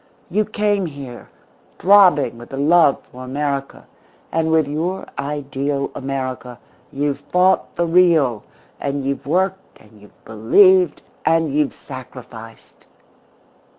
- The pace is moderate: No, slow, 120 wpm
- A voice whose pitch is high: No, medium, 145 Hz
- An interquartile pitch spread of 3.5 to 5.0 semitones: Yes, average, 4.7 semitones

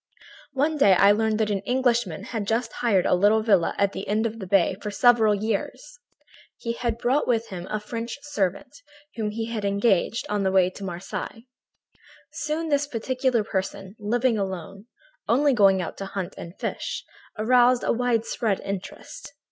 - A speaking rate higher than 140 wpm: Yes, average, 170 wpm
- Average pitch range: Yes, average, 3.6 semitones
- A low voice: No, high, 220 Hz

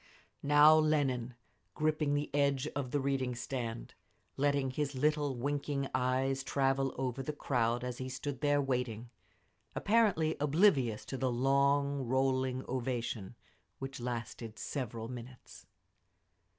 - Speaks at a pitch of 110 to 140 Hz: Yes, low, 135 Hz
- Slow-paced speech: Yes, slow, 125 wpm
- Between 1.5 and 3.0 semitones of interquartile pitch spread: Yes, narrow, 2.4 semitones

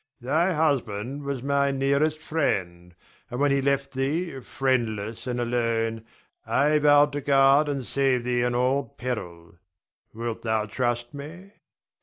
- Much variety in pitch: No, average, 3.3 semitones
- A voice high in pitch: No, low, 135 Hz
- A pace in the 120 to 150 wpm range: Yes, average, 140 wpm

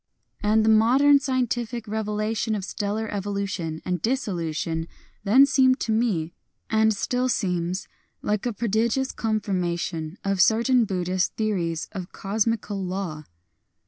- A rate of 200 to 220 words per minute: No, slow, 135 wpm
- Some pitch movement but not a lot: Yes, average, 3.8 semitones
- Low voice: No, high, 210 Hz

